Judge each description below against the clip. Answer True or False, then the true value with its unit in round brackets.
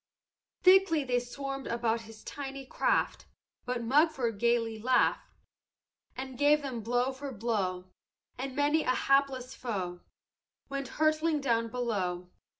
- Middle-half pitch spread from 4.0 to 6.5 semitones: False (3.4 semitones)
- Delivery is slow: True (125 wpm)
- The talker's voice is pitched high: True (255 Hz)